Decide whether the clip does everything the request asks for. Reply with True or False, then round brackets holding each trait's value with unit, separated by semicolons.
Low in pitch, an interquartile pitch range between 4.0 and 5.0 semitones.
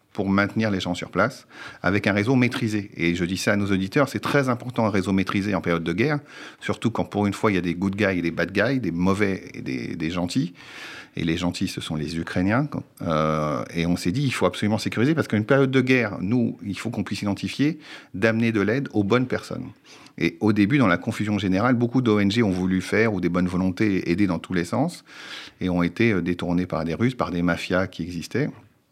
True (100 Hz; 4.3 semitones)